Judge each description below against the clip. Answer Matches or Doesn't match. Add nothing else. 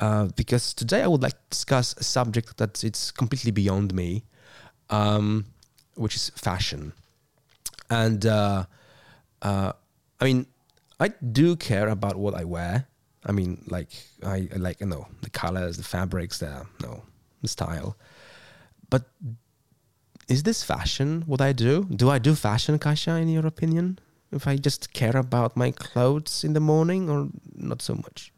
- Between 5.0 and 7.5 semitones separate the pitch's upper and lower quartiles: Matches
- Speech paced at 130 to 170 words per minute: Matches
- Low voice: Matches